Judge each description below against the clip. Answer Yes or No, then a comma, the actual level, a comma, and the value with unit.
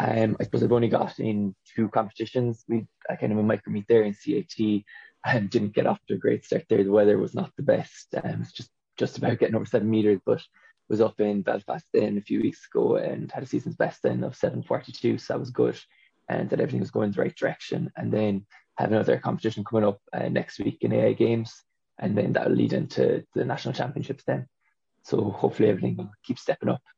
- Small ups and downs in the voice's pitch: Yes, narrow, 1.7 semitones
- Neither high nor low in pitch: No, low, 105 Hz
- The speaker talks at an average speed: No, fast, 230 wpm